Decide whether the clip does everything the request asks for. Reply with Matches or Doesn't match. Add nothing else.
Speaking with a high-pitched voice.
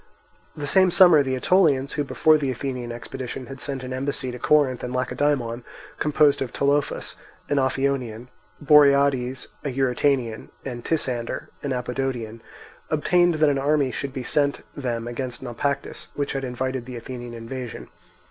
Doesn't match